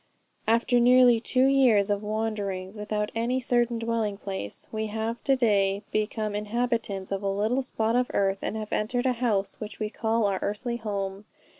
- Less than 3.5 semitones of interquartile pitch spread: Yes, average, 2.7 semitones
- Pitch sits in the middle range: No, high, 220 Hz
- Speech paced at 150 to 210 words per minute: Yes, average, 175 wpm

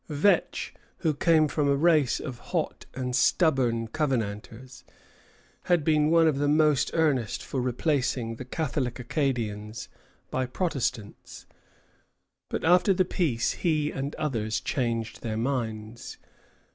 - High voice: No, low, 135 Hz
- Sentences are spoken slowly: Yes, slow, 125 wpm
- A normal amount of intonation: Yes, average, 4.8 semitones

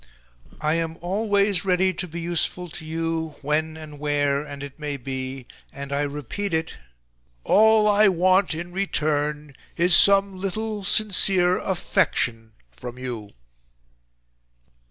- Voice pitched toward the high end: No, medium, 165 Hz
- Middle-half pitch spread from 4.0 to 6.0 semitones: Yes, average, 4.6 semitones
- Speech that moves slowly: Yes, slow, 130 wpm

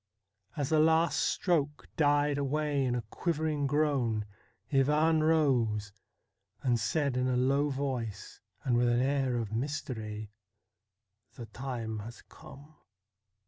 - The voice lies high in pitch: No, low, 135 Hz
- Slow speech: Yes, slow, 130 wpm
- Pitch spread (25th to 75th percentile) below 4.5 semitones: Yes, average, 4.1 semitones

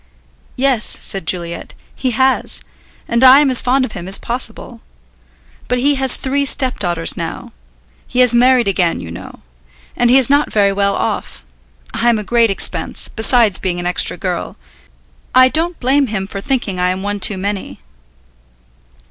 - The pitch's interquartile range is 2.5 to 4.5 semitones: No, average, 4.9 semitones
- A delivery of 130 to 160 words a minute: No, average, 170 wpm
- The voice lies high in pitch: Yes, high, 235 Hz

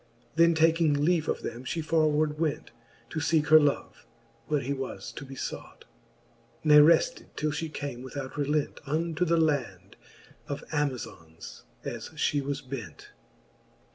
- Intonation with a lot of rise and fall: No, narrow, 2.6 semitones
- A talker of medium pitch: Yes, medium, 150 Hz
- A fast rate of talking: No, average, 145 wpm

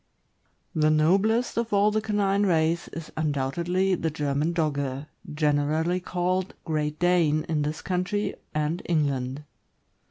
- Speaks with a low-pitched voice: No, medium, 160 Hz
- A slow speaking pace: Yes, slow, 125 wpm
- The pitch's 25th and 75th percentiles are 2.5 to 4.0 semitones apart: Yes, average, 3.6 semitones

